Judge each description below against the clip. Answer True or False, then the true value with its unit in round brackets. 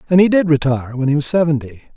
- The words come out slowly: False (245 wpm)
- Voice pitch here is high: False (150 Hz)